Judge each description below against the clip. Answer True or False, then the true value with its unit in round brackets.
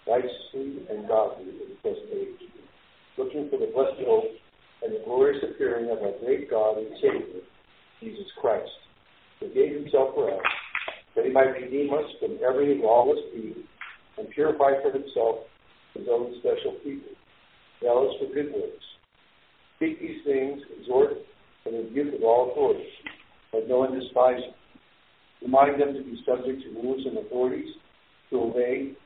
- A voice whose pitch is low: False (385 Hz)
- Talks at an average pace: True (155 wpm)